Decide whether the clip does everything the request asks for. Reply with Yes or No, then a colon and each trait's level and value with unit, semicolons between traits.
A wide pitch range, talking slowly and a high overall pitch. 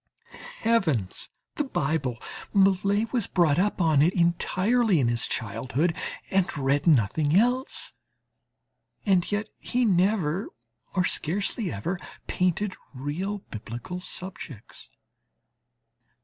No: wide, 5.8 semitones; slow, 105 wpm; medium, 180 Hz